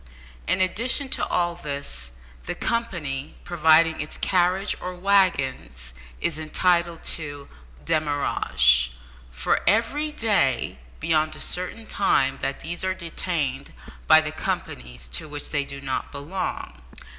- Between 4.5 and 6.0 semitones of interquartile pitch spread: Yes, average, 5.0 semitones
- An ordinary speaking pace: No, slow, 125 wpm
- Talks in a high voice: No, medium, 155 Hz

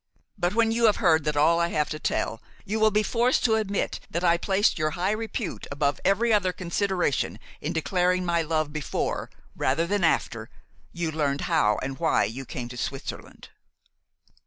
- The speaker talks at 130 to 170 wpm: No, average, 180 wpm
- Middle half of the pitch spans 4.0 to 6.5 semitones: Yes, average, 5.1 semitones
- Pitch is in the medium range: Yes, medium, 170 Hz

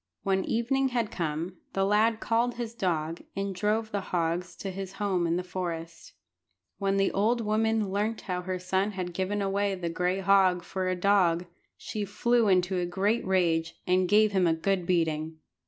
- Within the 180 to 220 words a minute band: Yes, average, 185 wpm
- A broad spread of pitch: No, average, 2.7 semitones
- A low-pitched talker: No, high, 190 Hz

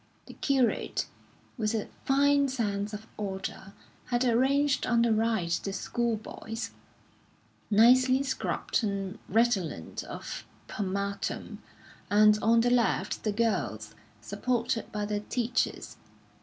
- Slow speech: Yes, slow, 115 wpm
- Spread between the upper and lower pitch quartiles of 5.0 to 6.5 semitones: No, average, 3.1 semitones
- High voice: Yes, high, 225 Hz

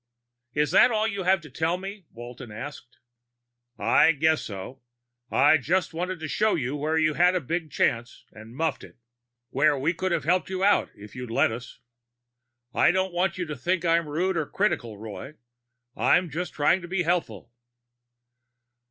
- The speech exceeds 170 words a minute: Yes, average, 180 wpm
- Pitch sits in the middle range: Yes, medium, 160 Hz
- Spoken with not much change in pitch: No, average, 5.2 semitones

